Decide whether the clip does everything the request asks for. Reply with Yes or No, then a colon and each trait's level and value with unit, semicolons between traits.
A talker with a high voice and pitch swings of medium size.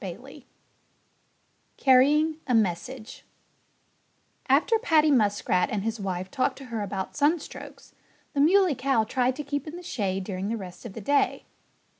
No: very high, 255 Hz; wide, 6.1 semitones